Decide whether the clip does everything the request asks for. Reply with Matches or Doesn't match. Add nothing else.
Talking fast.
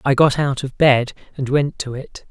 Matches